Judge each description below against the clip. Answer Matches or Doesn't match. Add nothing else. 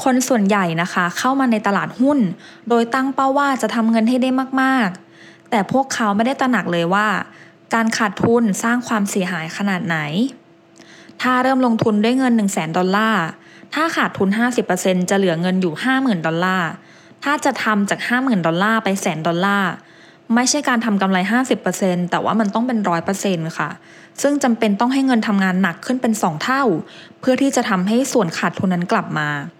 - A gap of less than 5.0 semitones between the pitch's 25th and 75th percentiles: Doesn't match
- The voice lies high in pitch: Matches